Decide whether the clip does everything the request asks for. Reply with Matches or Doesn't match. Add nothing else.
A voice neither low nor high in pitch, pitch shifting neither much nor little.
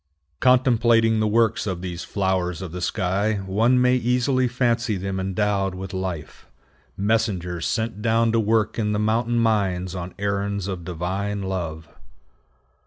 Doesn't match